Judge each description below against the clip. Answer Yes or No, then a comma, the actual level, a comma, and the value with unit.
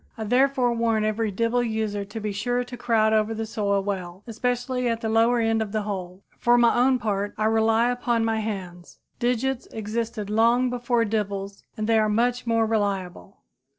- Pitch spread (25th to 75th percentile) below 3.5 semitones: Yes, narrow, 2.4 semitones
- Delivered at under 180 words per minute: No, average, 185 wpm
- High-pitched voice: Yes, high, 225 Hz